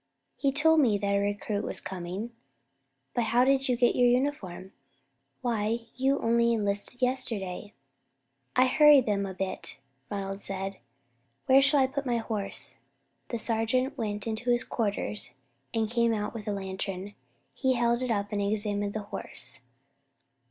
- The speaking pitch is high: Yes, high, 225 Hz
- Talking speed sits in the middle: Yes, average, 160 wpm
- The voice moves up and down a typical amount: Yes, average, 3.7 semitones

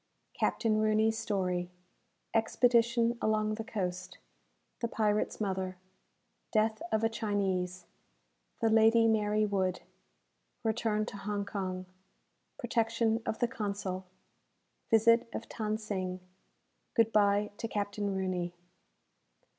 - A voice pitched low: No, high, 215 Hz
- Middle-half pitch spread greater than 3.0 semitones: No, narrow, 2.5 semitones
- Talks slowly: Yes, slow, 105 wpm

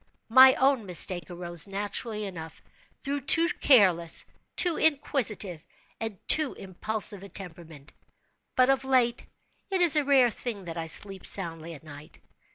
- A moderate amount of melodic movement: No, wide, 7.3 semitones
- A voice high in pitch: Yes, high, 205 Hz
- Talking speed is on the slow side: No, average, 145 wpm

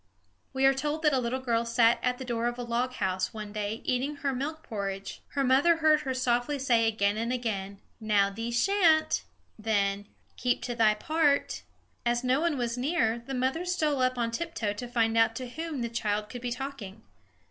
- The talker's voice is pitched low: No, high, 245 Hz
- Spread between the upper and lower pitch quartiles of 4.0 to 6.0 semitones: No, average, 3.5 semitones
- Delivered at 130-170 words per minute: No, average, 200 wpm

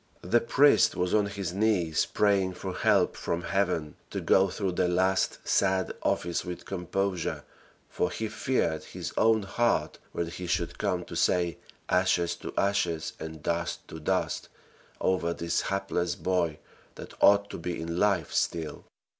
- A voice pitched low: Yes, very low, 90 Hz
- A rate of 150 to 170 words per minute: Yes, average, 155 wpm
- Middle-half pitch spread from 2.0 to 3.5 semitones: Yes, average, 2.8 semitones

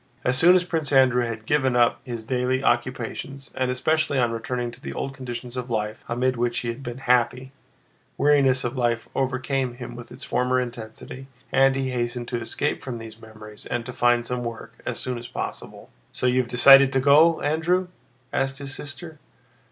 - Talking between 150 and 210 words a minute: Yes, average, 190 wpm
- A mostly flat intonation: Yes, narrow, 2.2 semitones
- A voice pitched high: No, low, 125 Hz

